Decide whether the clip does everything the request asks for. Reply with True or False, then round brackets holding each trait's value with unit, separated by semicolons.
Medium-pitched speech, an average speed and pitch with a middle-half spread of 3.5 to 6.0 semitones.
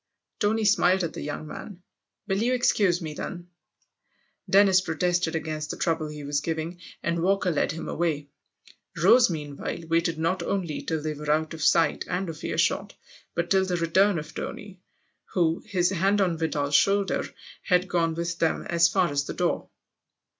False (170 Hz; 175 wpm; 3.0 semitones)